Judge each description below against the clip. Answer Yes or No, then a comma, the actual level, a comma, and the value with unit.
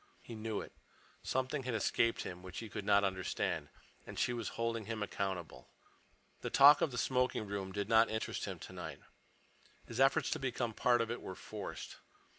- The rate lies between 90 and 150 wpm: No, average, 190 wpm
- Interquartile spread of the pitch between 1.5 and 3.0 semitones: No, average, 3.4 semitones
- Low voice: Yes, low, 115 Hz